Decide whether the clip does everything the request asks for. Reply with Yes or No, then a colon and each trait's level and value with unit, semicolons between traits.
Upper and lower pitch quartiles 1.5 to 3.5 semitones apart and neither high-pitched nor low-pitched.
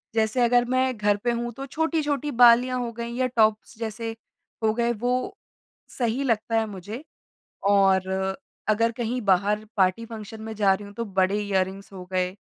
No: average, 3.1 semitones; high, 225 Hz